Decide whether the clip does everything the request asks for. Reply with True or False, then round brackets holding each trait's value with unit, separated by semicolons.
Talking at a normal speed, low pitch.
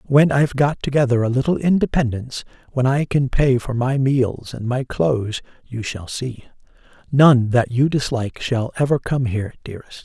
True (175 wpm; 130 Hz)